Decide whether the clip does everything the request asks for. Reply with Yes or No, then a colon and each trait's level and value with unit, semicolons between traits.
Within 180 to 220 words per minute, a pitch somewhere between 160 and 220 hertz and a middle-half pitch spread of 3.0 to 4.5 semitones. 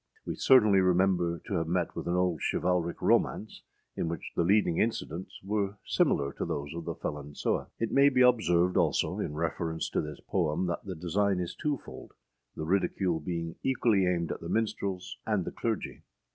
No: average, 185 wpm; very low, 90 Hz; average, 3.3 semitones